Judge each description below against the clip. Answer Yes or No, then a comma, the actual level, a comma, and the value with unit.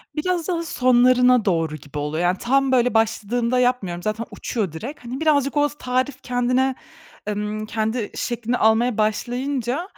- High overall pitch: Yes, high, 245 Hz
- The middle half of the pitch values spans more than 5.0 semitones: No, average, 3.4 semitones